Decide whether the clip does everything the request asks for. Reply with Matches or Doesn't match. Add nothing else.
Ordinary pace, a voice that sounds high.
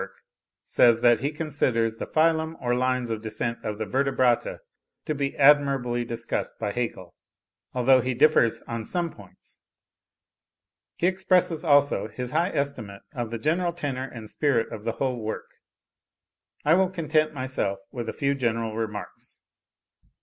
Doesn't match